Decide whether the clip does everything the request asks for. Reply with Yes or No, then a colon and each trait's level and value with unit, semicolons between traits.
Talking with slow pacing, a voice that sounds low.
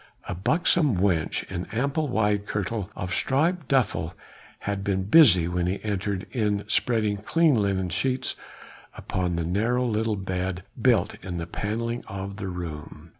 No: average, 150 wpm; low, 100 Hz